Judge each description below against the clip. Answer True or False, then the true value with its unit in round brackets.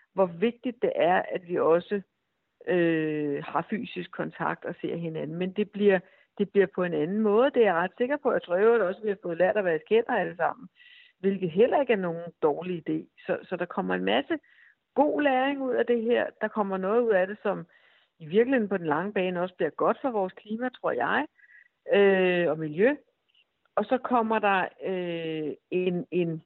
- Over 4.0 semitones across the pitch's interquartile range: True (5.6 semitones)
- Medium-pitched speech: False (195 Hz)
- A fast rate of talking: False (215 wpm)